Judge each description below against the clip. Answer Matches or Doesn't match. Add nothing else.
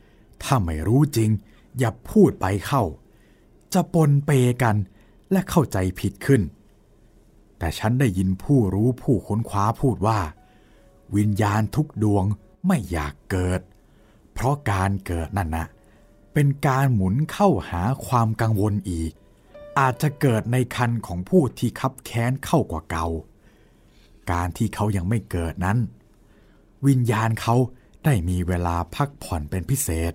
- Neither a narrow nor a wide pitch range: Doesn't match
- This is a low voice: Matches